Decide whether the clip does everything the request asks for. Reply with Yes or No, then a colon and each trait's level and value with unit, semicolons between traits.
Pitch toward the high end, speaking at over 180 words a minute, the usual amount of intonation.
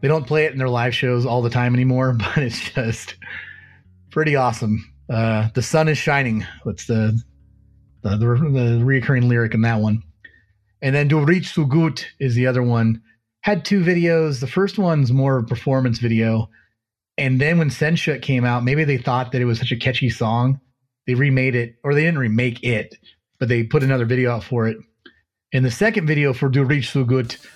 No: low, 125 Hz; average, 200 wpm; average, 3.5 semitones